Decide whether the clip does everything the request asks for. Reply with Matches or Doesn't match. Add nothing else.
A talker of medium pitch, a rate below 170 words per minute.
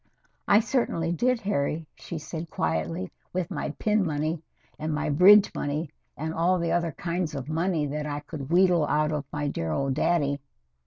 Doesn't match